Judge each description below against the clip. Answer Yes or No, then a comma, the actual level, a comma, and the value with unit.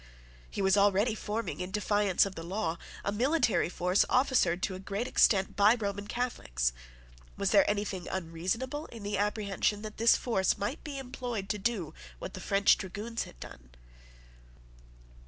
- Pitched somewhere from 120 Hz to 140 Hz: No, high, 205 Hz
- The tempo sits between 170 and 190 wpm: No, average, 160 wpm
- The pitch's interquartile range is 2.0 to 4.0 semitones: Yes, average, 3.3 semitones